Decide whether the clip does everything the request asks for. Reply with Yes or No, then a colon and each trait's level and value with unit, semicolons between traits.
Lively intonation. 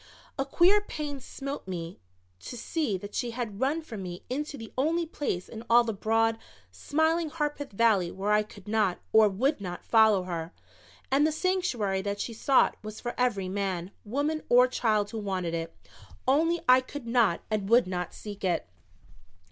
Yes: wide, 6.2 semitones